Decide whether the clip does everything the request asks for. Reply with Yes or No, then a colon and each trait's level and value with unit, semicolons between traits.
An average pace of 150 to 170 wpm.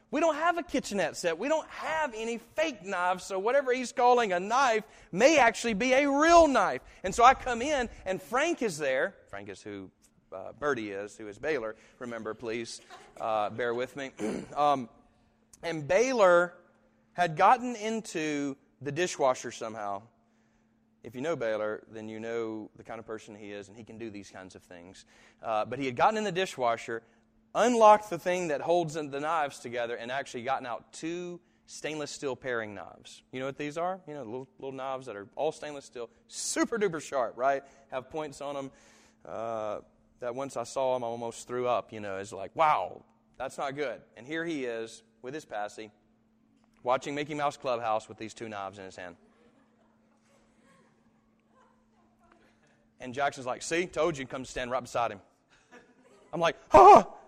No: average, 185 wpm